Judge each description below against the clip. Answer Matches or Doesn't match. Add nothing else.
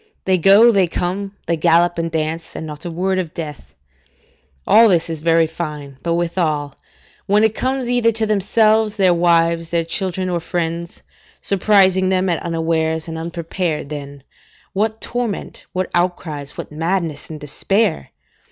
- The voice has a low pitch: Doesn't match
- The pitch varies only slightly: Doesn't match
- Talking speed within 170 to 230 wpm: Doesn't match